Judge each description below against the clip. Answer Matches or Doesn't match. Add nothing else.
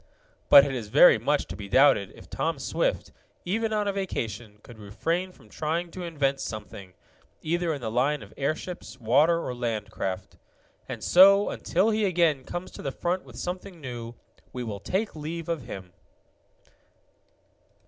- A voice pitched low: Doesn't match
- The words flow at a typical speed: Matches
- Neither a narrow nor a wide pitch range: Doesn't match